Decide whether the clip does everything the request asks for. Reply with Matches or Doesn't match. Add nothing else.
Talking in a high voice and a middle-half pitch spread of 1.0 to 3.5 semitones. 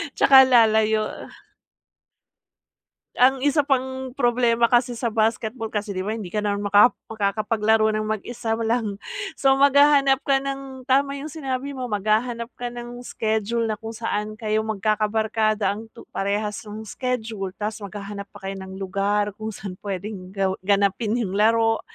Matches